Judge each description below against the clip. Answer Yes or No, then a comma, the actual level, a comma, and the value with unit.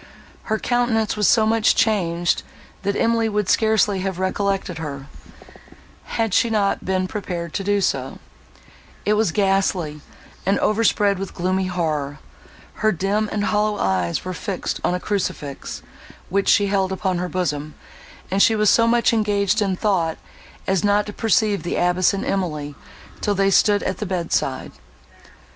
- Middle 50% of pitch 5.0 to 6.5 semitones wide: No, average, 2.8 semitones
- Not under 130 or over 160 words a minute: Yes, average, 155 wpm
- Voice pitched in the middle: No, high, 195 Hz